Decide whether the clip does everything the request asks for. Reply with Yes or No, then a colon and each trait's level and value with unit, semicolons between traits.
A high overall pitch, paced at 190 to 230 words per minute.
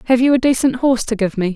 No: high, 240 Hz; fast, 310 wpm